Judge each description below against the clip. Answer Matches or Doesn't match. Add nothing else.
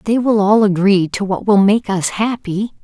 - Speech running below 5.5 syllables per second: Matches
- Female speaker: Matches